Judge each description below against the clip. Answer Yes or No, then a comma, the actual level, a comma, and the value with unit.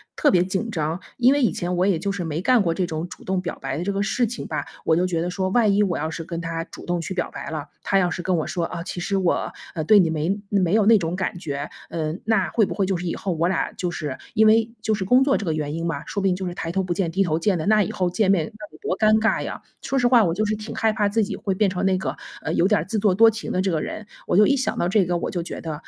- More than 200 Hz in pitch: No, medium, 185 Hz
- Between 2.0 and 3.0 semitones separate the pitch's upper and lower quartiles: No, average, 3.9 semitones